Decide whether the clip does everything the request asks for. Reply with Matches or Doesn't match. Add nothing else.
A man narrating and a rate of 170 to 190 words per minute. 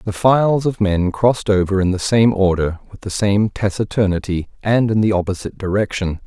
Matches